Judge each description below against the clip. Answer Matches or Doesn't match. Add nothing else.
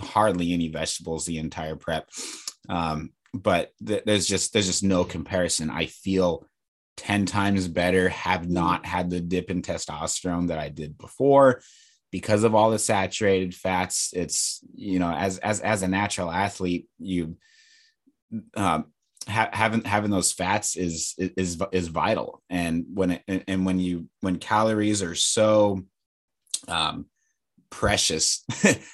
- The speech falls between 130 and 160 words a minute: Matches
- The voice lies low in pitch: Matches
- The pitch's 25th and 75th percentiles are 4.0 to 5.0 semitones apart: Doesn't match